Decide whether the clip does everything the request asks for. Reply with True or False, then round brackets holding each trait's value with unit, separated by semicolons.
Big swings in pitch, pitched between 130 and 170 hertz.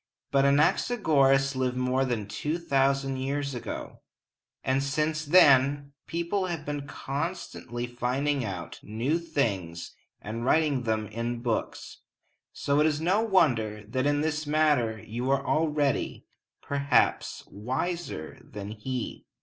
False (4.1 semitones; 135 Hz)